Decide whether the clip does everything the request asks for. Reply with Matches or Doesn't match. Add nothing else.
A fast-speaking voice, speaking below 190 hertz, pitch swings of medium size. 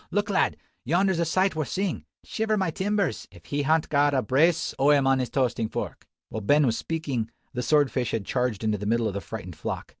Doesn't match